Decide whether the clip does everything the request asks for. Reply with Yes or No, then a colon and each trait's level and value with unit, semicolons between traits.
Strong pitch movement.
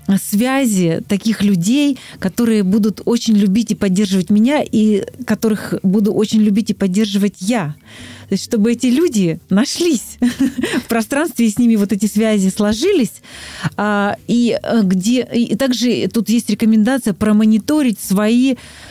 No: average, 2.8 semitones